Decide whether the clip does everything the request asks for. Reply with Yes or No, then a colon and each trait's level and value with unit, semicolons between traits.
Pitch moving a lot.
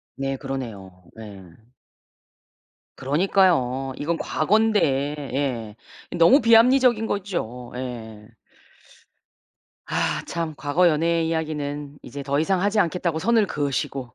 Yes: wide, 5.8 semitones